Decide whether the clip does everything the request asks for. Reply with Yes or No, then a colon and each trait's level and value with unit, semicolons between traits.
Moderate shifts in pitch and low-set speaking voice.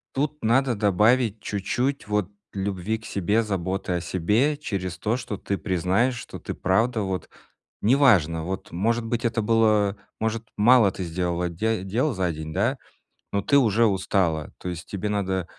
Yes: average, 3.8 semitones; low, 105 Hz